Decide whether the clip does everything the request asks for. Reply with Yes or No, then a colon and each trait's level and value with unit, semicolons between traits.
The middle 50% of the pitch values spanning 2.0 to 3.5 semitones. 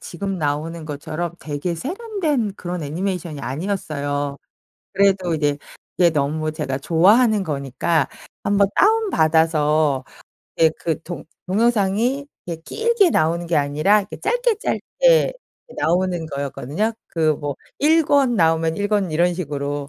No: average, 5.2 semitones